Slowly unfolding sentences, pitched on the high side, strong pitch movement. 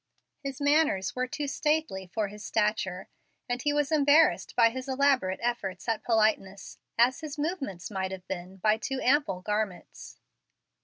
No: average, 155 wpm; high, 230 Hz; wide, 6.8 semitones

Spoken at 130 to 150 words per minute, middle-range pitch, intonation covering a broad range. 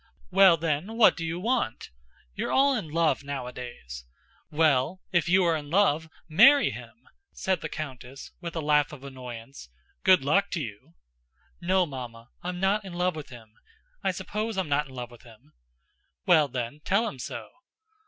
No: average, 175 wpm; medium, 155 Hz; wide, 6.2 semitones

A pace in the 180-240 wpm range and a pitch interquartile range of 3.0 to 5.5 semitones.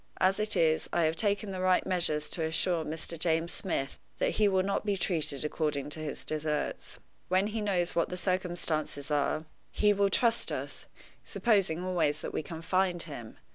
Yes: average, 185 wpm; average, 3.4 semitones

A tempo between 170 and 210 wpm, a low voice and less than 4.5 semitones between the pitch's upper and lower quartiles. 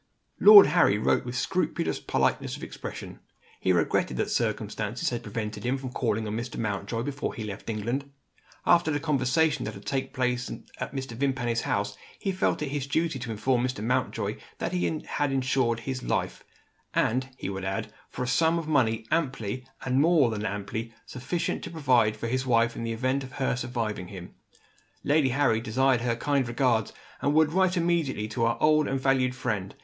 Yes: average, 185 wpm; low, 125 Hz; average, 3.9 semitones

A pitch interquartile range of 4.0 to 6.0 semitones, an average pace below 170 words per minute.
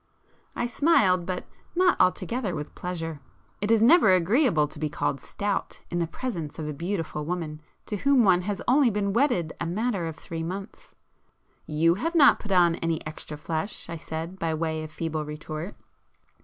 No: average, 4.7 semitones; average, 180 wpm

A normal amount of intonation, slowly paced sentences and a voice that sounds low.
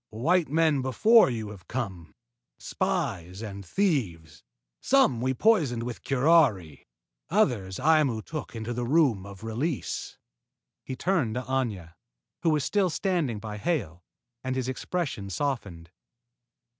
No: wide, 7.3 semitones; slow, 130 wpm; low, 125 Hz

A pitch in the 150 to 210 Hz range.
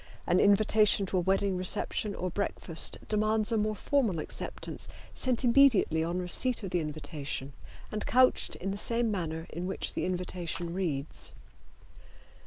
Yes: high, 190 Hz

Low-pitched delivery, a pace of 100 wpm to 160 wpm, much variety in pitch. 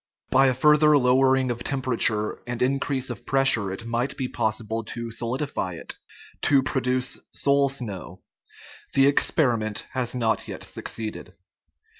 No: low, 125 Hz; average, 145 wpm; average, 2.9 semitones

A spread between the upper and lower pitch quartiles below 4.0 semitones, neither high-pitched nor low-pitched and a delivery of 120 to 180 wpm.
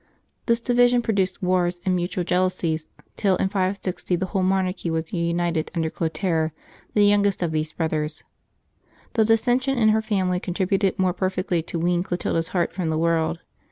Yes: average, 2.8 semitones; medium, 180 Hz; average, 165 wpm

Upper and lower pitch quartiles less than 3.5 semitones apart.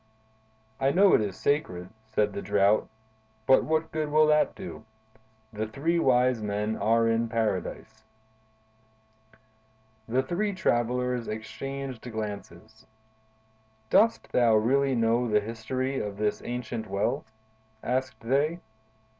No: average, 4.0 semitones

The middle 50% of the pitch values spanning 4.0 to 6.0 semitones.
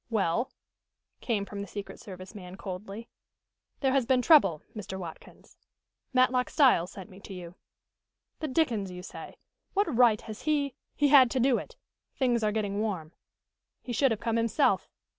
Yes: average, 4.9 semitones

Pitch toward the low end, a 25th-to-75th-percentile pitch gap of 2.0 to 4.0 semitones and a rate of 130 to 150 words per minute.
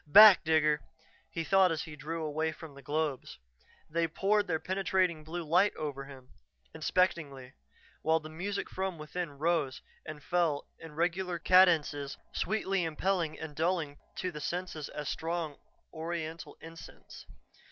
No: medium, 160 Hz; average, 2.8 semitones; average, 140 wpm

